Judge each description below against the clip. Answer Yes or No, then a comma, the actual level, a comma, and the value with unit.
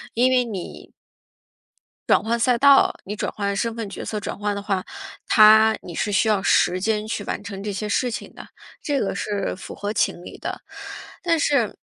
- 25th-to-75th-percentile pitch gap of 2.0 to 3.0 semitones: Yes, narrow, 2.6 semitones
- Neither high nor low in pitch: No, high, 215 Hz